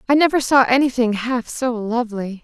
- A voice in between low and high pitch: No, high, 245 Hz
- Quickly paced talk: No, average, 195 wpm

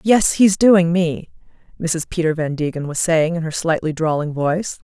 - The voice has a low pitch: No, medium, 165 Hz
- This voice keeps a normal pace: Yes, average, 170 wpm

